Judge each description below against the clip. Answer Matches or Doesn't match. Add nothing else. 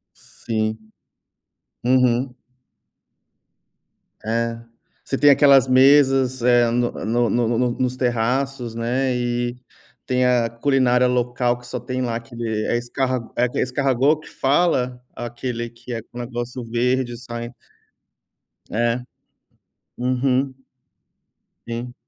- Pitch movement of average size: Doesn't match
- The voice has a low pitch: Matches